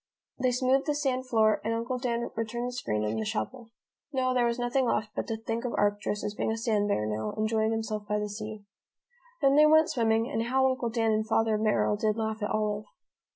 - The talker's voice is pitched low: No, high, 225 Hz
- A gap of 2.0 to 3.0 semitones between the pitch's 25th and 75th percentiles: Yes, narrow, 2.6 semitones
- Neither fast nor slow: No, fast, 225 wpm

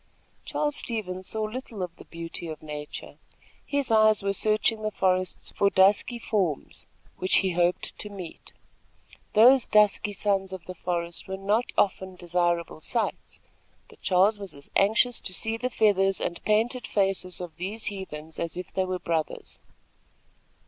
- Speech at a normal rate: Yes, average, 155 wpm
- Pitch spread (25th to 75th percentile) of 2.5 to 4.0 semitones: Yes, average, 3.2 semitones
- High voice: Yes, high, 195 Hz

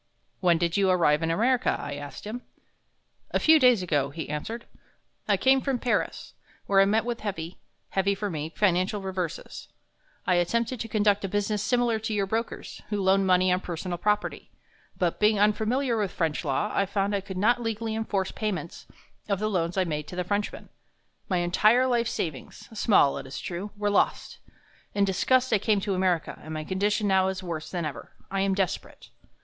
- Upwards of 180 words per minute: Yes, average, 190 wpm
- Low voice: No, high, 195 Hz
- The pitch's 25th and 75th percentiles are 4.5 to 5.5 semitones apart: No, average, 3.4 semitones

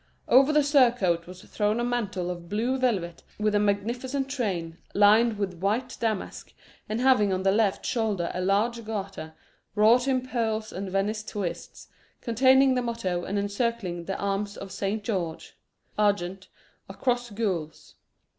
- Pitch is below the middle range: No, high, 210 Hz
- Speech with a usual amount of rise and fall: Yes, average, 3.8 semitones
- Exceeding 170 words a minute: No, average, 155 wpm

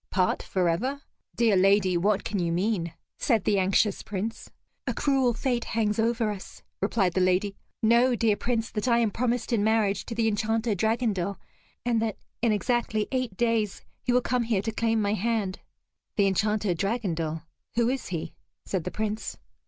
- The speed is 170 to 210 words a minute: Yes, average, 175 wpm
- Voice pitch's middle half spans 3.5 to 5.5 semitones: No, average, 3.1 semitones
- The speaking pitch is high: Yes, high, 215 Hz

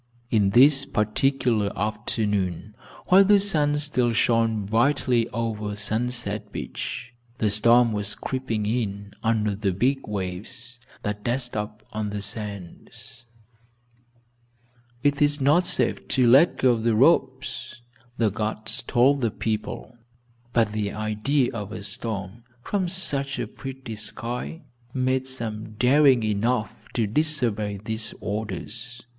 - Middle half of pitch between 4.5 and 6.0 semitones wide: No, average, 3.7 semitones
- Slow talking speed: Yes, slow, 125 wpm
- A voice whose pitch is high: No, low, 115 Hz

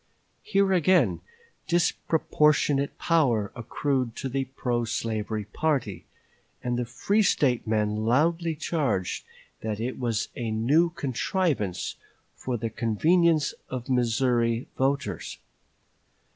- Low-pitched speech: Yes, low, 130 Hz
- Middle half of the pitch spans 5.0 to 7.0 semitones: Yes, wide, 5.6 semitones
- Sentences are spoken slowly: Yes, slow, 105 wpm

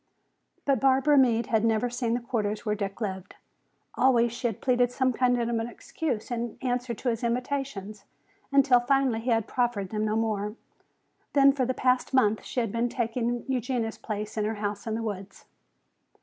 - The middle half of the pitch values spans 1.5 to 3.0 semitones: Yes, average, 2.7 semitones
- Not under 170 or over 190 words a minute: Yes, average, 185 wpm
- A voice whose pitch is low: No, high, 235 Hz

